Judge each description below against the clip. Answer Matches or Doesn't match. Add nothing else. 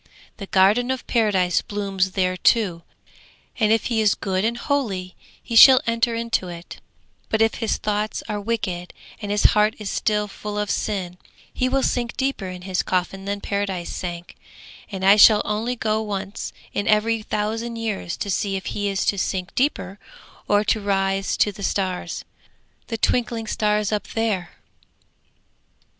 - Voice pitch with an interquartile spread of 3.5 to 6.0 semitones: Doesn't match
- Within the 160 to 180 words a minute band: Matches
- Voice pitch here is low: Doesn't match